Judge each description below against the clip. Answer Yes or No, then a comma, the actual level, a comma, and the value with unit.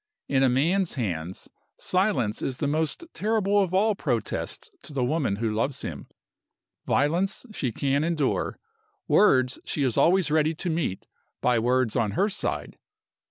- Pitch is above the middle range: No, medium, 145 Hz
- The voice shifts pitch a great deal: Yes, wide, 6.5 semitones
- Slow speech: No, average, 155 wpm